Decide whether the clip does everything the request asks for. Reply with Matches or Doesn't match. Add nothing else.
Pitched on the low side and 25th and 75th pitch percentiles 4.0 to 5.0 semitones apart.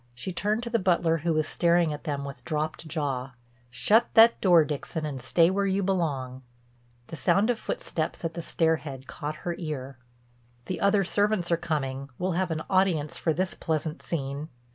Doesn't match